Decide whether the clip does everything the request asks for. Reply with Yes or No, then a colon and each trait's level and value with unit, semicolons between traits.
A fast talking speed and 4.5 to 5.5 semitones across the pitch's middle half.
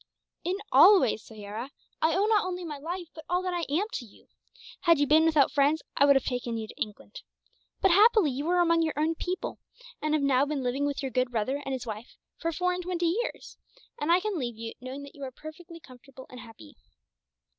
Yes: fast, 230 wpm; average, 5.2 semitones